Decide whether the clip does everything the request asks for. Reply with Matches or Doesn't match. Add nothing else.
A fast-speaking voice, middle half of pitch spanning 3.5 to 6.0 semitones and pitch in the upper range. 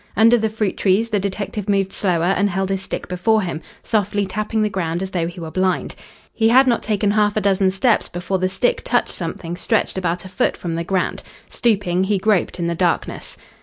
Doesn't match